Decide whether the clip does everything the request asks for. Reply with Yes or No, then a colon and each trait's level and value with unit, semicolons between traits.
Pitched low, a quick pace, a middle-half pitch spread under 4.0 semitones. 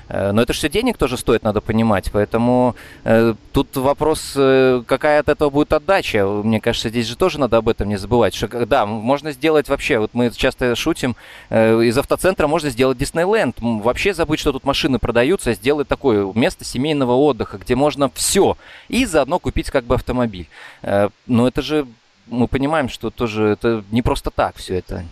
No: low, 125 Hz; fast, 185 wpm; average, 4.5 semitones